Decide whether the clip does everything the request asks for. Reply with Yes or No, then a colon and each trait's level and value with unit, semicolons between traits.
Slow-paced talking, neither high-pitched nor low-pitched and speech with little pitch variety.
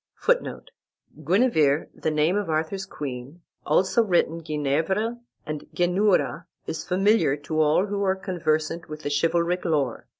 No: slow, 130 wpm; medium, 170 Hz; average, 3.9 semitones